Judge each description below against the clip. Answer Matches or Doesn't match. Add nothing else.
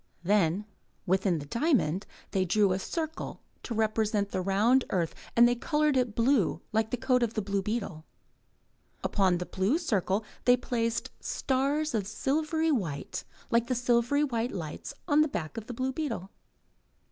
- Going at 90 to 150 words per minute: Doesn't match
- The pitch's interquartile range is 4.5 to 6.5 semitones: Matches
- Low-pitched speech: Doesn't match